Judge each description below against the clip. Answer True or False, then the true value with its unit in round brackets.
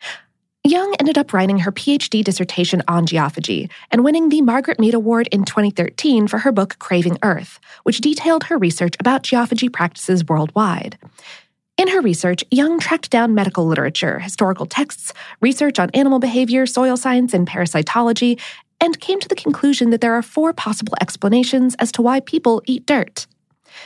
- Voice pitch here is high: True (235 Hz)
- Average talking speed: True (165 wpm)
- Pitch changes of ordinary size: False (6.9 semitones)